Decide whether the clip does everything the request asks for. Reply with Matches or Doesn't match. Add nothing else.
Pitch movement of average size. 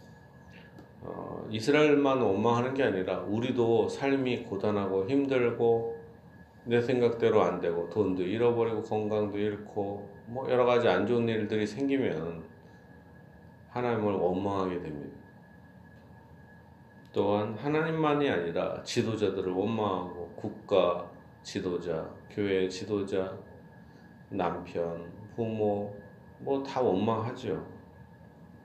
Matches